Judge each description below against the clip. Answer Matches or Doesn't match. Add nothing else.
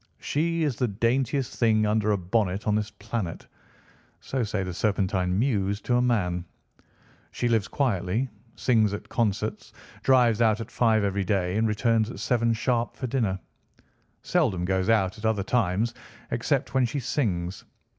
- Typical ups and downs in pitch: Matches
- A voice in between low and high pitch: Doesn't match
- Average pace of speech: Matches